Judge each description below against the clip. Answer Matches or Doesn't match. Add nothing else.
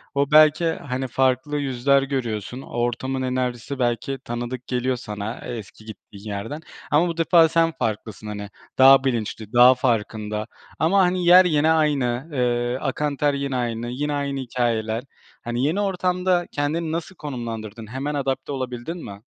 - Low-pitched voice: Matches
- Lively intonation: Doesn't match